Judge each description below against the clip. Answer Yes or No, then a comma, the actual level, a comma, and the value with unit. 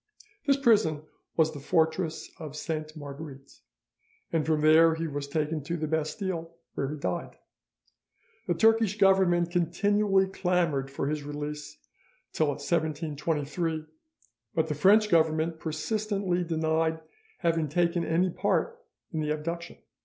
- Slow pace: Yes, slow, 130 wpm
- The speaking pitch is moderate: Yes, medium, 160 Hz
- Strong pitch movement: No, narrow, 2.6 semitones